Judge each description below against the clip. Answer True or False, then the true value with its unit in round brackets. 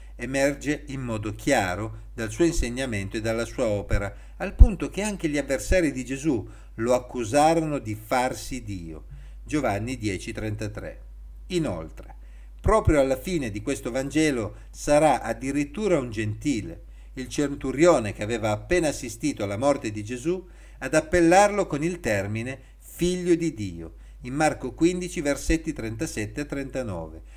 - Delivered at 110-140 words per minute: True (130 wpm)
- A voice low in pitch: True (130 Hz)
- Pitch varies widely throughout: True (5.8 semitones)